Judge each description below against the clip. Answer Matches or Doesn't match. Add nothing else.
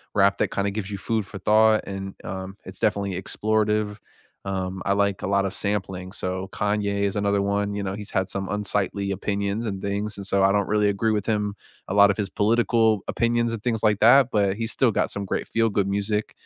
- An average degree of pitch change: Doesn't match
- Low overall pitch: Matches